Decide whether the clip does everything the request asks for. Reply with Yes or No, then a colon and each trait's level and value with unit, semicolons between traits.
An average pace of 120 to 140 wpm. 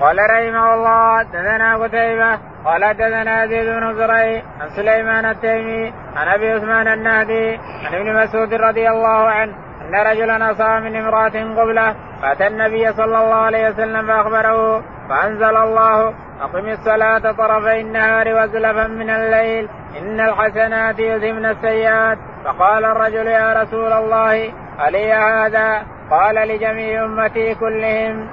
Yes: average, 125 wpm